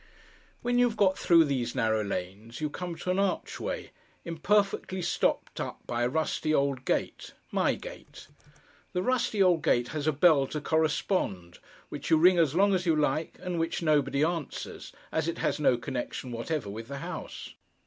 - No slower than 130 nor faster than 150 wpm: No, average, 175 wpm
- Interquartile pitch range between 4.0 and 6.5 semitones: Yes, wide, 5.6 semitones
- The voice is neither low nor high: Yes, medium, 155 Hz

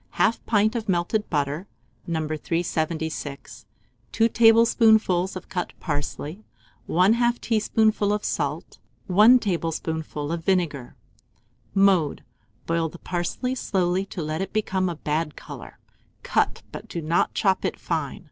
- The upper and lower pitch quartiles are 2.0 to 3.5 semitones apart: No, average, 4.9 semitones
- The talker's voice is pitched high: No, medium, 175 Hz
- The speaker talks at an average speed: No, slow, 130 wpm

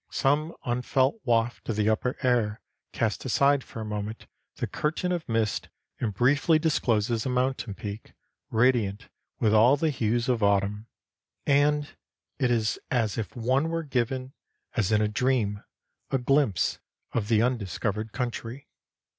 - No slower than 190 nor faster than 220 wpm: No, average, 145 wpm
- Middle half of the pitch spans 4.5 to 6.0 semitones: No, average, 3.7 semitones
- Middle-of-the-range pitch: No, low, 120 Hz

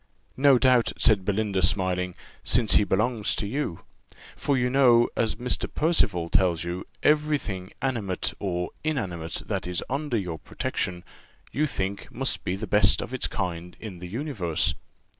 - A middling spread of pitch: No, wide, 5.8 semitones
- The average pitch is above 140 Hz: No, low, 100 Hz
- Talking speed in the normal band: Yes, average, 160 wpm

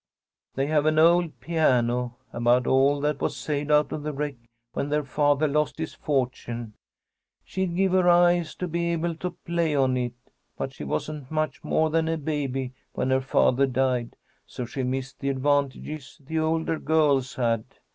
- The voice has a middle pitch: Yes, medium, 145 Hz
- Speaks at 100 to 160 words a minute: No, average, 175 wpm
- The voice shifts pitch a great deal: No, average, 3.3 semitones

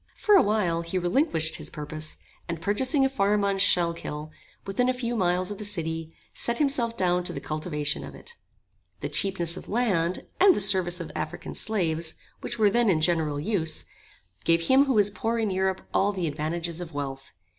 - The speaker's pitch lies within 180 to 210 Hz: Yes, medium, 185 Hz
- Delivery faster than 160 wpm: Yes, average, 190 wpm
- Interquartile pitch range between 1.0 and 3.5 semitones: No, average, 4.8 semitones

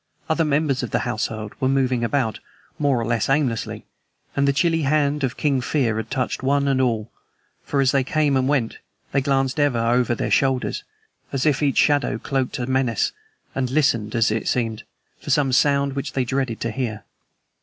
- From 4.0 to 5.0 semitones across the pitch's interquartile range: No, average, 3.0 semitones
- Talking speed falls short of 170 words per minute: No, average, 190 wpm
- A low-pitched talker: Yes, low, 130 Hz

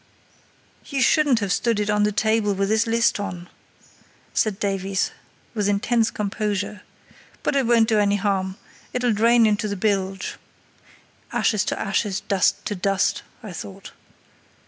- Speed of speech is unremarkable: Yes, average, 145 wpm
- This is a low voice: No, high, 210 Hz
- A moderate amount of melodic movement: No, narrow, 2.3 semitones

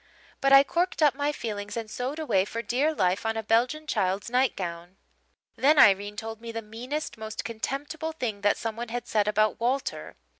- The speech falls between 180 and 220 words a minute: Yes, average, 185 wpm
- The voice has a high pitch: Yes, high, 230 Hz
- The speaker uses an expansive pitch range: No, average, 4.6 semitones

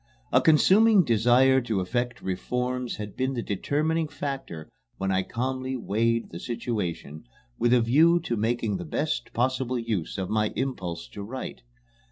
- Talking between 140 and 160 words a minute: Yes, average, 155 wpm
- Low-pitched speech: Yes, low, 120 Hz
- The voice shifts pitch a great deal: No, average, 4.3 semitones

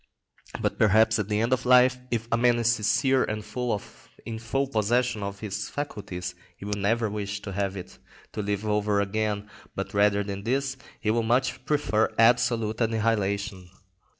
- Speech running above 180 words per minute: No, average, 170 wpm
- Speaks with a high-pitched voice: No, low, 110 Hz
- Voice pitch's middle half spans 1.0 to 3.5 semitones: Yes, average, 2.7 semitones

